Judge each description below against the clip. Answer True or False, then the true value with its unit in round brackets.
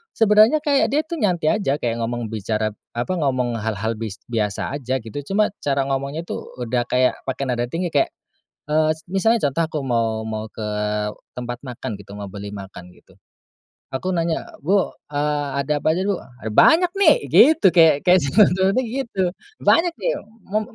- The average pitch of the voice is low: False (145 Hz)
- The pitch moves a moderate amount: False (8.3 semitones)